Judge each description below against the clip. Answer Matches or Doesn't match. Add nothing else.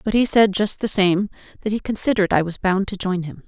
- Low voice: Doesn't match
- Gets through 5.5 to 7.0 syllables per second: Matches